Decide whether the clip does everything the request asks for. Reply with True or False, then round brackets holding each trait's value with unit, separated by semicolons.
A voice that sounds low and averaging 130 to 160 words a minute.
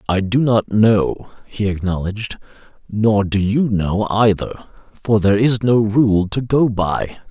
True (105 Hz; 155 wpm)